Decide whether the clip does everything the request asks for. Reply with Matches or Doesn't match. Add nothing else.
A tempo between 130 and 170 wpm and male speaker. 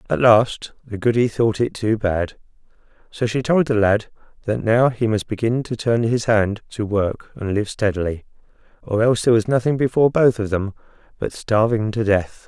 Doesn't match